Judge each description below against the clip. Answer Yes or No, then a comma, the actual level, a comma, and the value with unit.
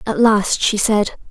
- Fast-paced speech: No, average, 185 wpm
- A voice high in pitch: Yes, high, 210 Hz